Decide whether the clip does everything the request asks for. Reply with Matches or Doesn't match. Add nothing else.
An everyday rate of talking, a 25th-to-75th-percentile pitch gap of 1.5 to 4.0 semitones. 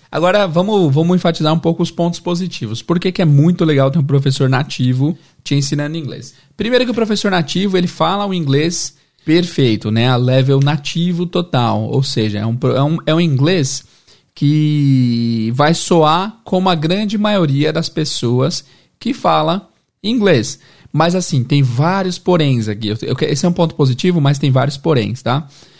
Doesn't match